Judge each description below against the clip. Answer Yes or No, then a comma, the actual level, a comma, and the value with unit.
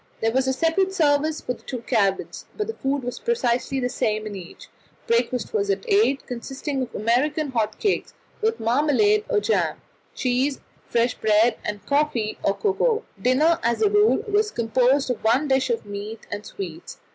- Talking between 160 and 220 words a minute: Yes, average, 180 wpm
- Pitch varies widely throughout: Yes, wide, 6.1 semitones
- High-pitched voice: Yes, very high, 260 Hz